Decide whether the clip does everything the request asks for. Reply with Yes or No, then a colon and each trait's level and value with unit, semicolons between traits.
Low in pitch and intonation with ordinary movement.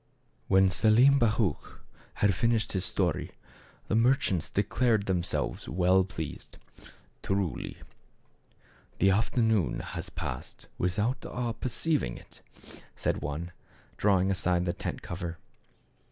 Yes: very low, 95 Hz; average, 4.2 semitones